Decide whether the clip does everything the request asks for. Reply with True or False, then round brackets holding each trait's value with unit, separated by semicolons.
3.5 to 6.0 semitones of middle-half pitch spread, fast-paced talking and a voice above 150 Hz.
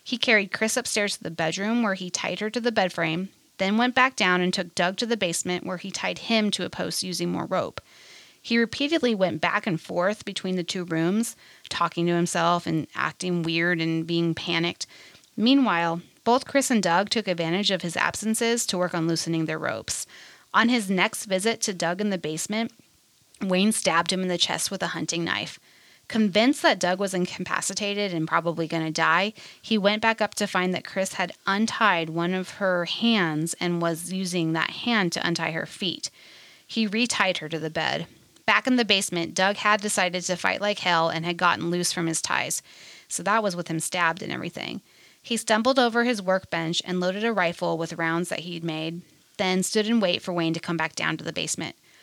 True (4.0 semitones; 210 wpm; 185 Hz)